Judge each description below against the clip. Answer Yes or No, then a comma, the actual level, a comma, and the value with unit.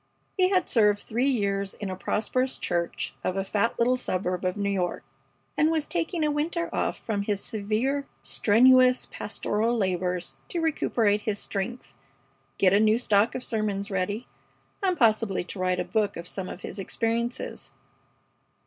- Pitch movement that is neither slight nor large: Yes, average, 4.4 semitones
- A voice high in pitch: Yes, high, 215 Hz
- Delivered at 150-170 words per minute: Yes, average, 165 wpm